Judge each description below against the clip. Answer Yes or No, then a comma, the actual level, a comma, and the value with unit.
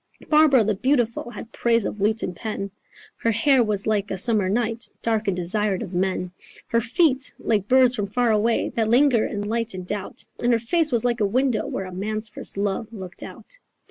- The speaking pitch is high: Yes, high, 220 Hz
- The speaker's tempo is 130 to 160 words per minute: No, fast, 205 wpm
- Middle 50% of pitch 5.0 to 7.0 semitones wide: No, average, 3.1 semitones